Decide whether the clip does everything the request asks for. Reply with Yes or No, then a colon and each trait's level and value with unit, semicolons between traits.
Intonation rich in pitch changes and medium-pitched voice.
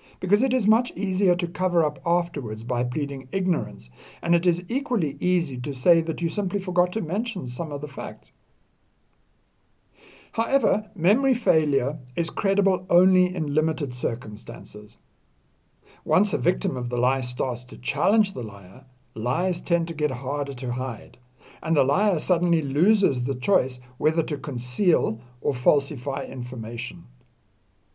Yes: wide, 6.4 semitones; medium, 155 Hz